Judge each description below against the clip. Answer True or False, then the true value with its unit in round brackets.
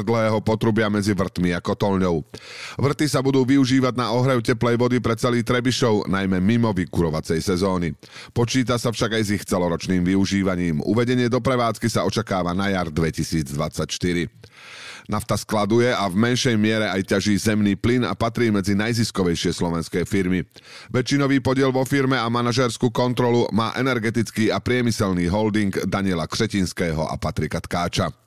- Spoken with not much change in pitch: False (4.6 semitones)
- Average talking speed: True (150 wpm)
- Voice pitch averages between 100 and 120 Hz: True (110 Hz)